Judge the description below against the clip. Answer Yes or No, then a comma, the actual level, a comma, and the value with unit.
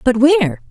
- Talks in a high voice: Yes, very high, 255 Hz